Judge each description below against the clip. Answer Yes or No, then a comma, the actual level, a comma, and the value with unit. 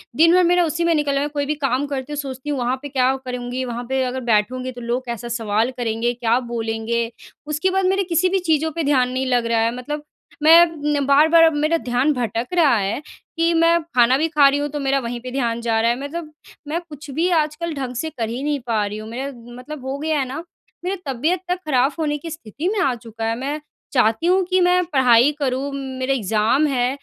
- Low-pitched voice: No, very high, 270 Hz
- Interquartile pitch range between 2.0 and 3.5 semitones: No, average, 4.1 semitones